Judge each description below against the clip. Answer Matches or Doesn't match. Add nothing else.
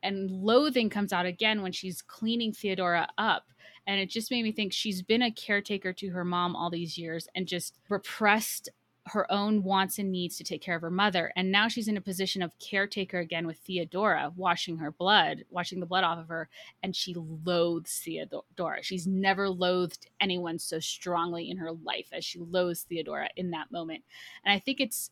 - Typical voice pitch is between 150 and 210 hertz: Matches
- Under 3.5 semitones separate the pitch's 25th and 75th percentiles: Matches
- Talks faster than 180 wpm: Matches